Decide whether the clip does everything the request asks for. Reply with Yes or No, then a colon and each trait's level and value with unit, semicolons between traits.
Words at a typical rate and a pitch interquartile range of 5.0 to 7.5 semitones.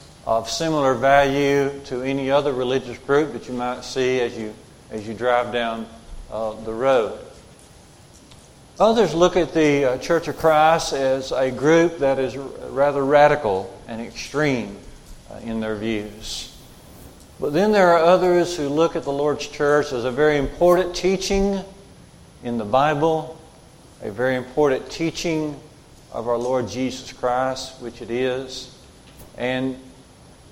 No: average, 145 wpm; average, 3.8 semitones